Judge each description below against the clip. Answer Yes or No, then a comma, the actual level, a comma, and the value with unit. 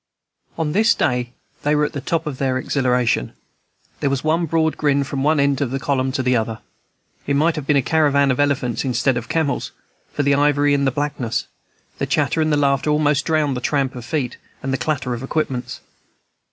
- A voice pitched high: No, medium, 140 Hz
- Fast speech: Yes, fast, 210 wpm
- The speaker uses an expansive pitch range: No, narrow, 2.5 semitones